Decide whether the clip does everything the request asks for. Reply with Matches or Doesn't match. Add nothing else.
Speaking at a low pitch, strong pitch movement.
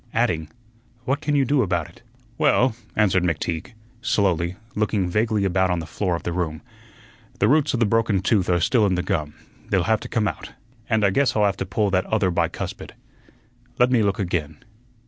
Doesn't match